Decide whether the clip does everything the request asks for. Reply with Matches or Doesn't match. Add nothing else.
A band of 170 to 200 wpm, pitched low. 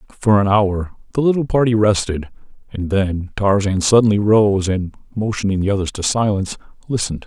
Doesn't match